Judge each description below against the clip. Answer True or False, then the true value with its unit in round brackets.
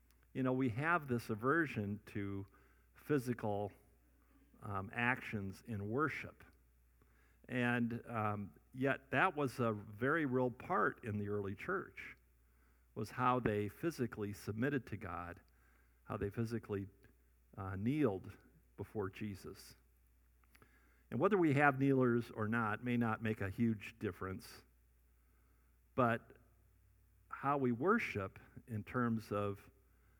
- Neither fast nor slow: False (115 wpm)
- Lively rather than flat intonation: True (5.8 semitones)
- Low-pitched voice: True (105 Hz)